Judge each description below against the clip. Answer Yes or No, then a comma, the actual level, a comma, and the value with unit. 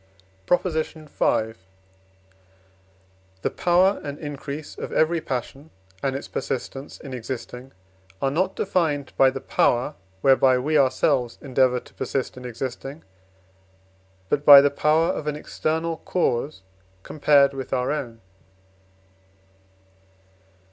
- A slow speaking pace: Yes, slow, 115 wpm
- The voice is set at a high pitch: No, medium, 140 Hz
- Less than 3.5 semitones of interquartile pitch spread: Yes, average, 3.1 semitones